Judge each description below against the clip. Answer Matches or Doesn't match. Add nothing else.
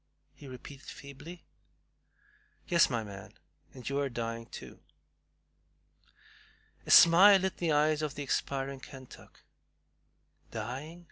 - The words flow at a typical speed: Doesn't match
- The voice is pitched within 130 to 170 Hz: Matches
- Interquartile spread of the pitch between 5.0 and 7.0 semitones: Doesn't match